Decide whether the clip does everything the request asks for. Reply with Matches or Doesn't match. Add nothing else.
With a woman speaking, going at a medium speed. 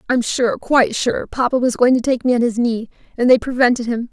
Doesn't match